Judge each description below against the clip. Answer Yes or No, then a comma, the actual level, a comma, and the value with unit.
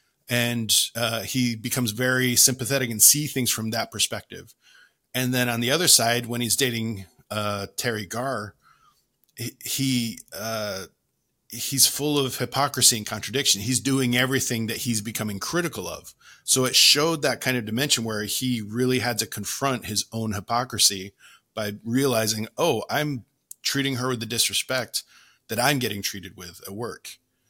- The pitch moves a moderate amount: Yes, average, 3.2 semitones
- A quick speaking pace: No, average, 155 wpm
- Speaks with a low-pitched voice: Yes, low, 120 Hz